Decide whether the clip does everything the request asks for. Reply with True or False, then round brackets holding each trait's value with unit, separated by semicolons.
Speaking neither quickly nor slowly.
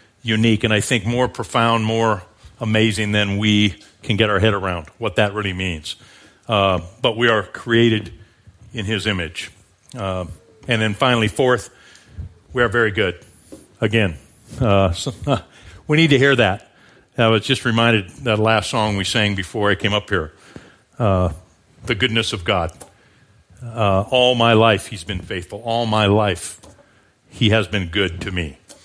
True (165 wpm)